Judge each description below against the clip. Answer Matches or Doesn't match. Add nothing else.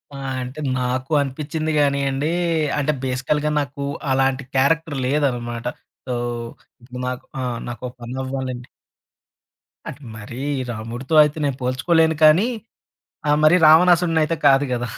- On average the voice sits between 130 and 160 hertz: Matches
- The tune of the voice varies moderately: Matches